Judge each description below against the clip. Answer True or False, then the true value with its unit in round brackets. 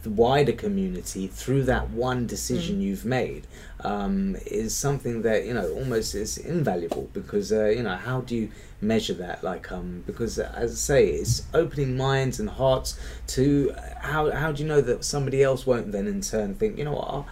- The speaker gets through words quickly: False (195 wpm)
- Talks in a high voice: False (125 Hz)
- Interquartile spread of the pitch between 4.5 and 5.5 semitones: True (5.2 semitones)